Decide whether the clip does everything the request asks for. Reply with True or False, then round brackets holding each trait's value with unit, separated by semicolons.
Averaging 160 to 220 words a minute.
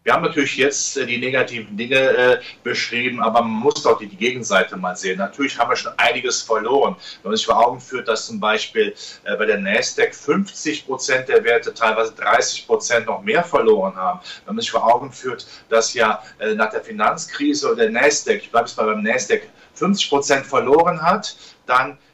True (190 wpm)